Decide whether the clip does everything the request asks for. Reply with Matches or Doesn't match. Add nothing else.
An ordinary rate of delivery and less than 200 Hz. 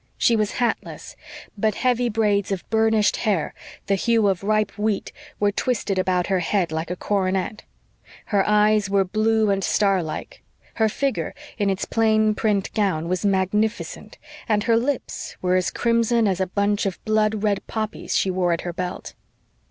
Doesn't match